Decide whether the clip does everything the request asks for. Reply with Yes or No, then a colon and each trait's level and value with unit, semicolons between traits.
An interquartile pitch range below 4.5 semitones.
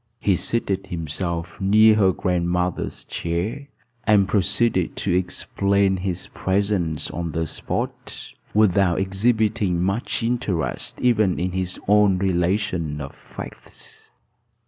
Yes: average, 2.9 semitones